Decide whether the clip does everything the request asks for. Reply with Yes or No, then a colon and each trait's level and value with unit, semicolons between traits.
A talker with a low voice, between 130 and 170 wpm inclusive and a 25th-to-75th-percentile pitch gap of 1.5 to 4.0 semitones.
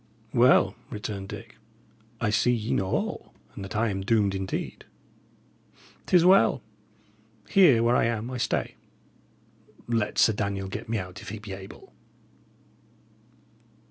Yes: low, 110 Hz; average, 140 wpm; average, 3.2 semitones